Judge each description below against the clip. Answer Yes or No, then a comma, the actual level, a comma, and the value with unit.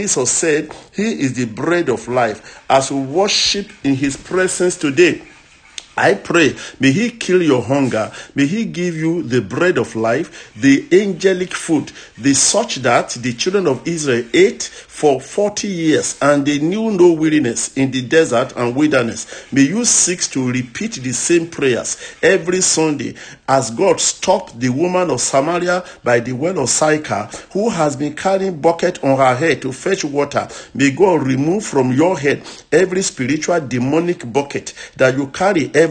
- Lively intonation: Yes, wide, 5.7 semitones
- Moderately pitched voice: Yes, medium, 160 Hz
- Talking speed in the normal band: Yes, average, 170 wpm